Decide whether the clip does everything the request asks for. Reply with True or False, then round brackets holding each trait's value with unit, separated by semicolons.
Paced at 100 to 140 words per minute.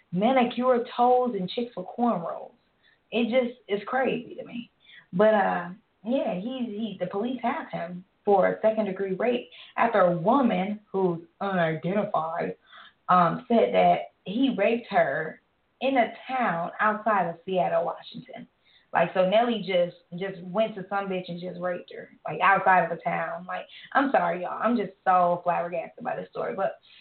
False (165 wpm)